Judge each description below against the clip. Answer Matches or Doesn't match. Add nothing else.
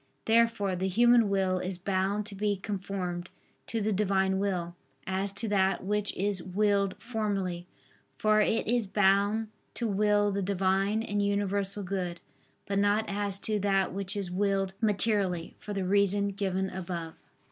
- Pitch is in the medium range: Doesn't match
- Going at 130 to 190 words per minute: Matches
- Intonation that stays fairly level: Matches